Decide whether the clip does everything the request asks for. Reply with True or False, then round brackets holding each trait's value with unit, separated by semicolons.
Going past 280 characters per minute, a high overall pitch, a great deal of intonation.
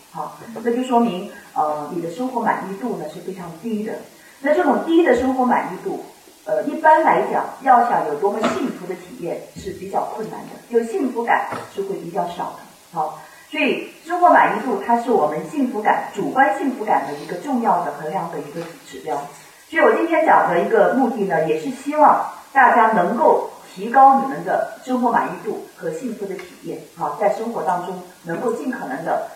True (290 characters per minute; 235 Hz; 7.5 semitones)